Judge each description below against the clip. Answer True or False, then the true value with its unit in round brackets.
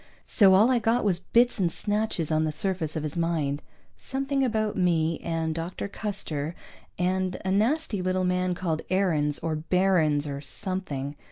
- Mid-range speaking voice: True (180 Hz)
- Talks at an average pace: True (165 wpm)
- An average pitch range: True (4.2 semitones)